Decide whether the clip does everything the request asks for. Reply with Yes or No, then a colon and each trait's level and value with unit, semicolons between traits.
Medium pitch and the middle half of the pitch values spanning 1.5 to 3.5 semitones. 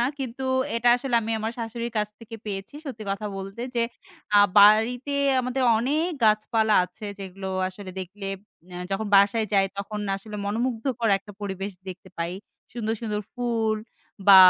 No: high, 220 Hz; average, 3.0 semitones